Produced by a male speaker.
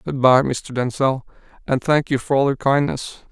Yes: male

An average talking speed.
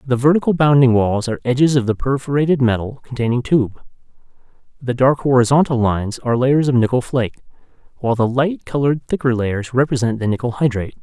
Yes: average, 170 wpm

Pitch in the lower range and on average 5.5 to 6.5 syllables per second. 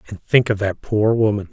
No: low, 105 Hz; 5.3 syllables/s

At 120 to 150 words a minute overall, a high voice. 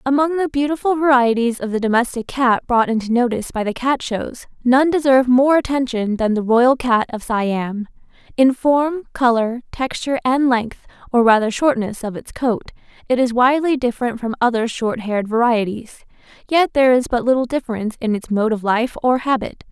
No: average, 180 wpm; high, 245 Hz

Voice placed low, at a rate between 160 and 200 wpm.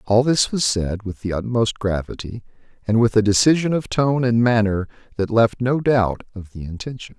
Yes: low, 110 Hz; average, 190 wpm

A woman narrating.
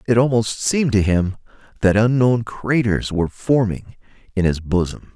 No: male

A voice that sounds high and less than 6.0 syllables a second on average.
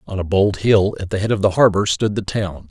No: low, 100 Hz; 5.5 syllables/s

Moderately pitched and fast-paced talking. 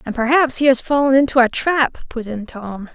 No: very high, 255 Hz; fast, 225 wpm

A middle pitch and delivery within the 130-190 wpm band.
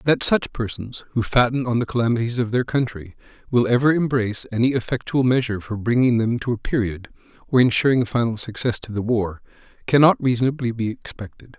No: low, 120 Hz; average, 175 wpm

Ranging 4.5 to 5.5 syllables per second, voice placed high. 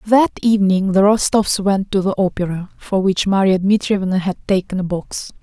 Yes: 5.2 syllables/s; high, 195 Hz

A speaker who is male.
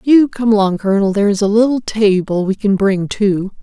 No: female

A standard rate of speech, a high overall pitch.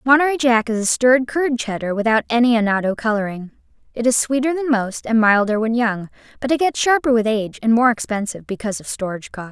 No: fast, 210 wpm; high, 235 Hz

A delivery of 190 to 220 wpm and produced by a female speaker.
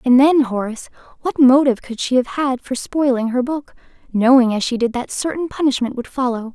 Yes: average, 200 wpm; female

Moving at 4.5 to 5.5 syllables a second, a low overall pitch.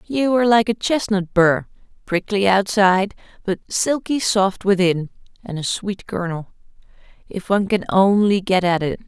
No: 4.7 syllables/s; high, 200 Hz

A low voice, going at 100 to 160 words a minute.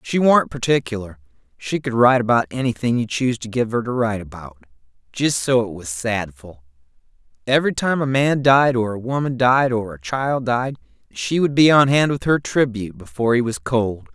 No: low, 120 Hz; average, 195 wpm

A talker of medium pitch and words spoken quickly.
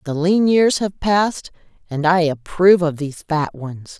No: medium, 170 Hz; average, 180 wpm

